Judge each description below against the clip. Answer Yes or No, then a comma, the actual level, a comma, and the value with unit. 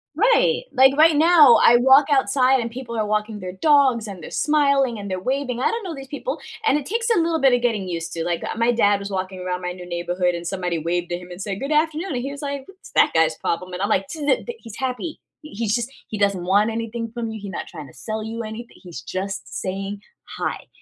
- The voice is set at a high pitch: Yes, high, 230 Hz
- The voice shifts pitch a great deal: Yes, wide, 6.9 semitones